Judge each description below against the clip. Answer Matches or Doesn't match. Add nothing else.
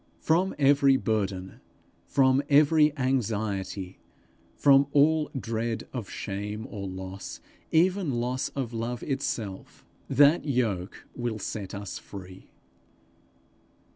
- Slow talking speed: Matches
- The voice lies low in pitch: Matches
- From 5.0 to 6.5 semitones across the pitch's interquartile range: Matches